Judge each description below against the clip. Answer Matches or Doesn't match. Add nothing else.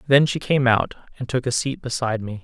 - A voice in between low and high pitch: Doesn't match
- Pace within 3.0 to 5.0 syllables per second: Doesn't match